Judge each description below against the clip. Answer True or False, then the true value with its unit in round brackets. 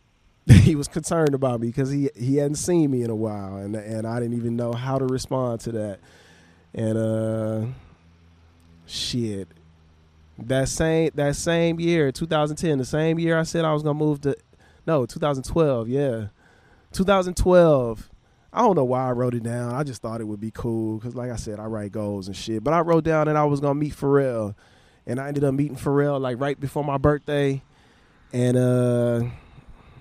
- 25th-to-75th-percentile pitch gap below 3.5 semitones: False (4.8 semitones)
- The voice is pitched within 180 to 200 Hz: False (125 Hz)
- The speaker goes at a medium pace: True (190 wpm)